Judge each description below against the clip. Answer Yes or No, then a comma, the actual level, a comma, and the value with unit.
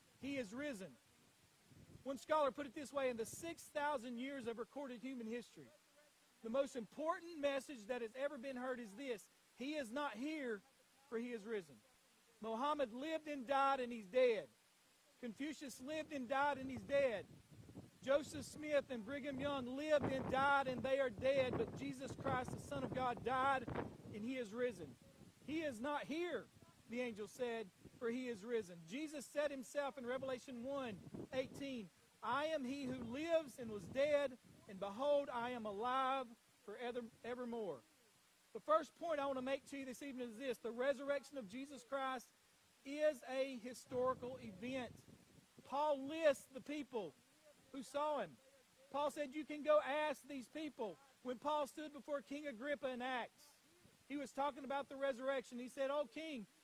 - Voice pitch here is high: Yes, very high, 270 Hz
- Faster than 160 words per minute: Yes, average, 170 wpm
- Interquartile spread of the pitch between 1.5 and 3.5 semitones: Yes, narrow, 2.6 semitones